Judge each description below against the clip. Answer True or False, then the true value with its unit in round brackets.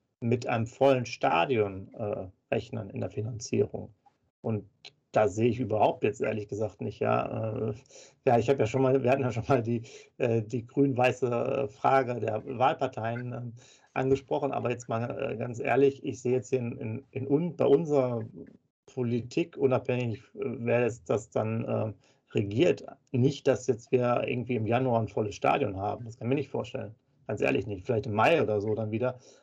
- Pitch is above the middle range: False (125 Hz)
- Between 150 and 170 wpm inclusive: False (185 wpm)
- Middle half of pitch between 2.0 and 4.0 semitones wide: True (3.1 semitones)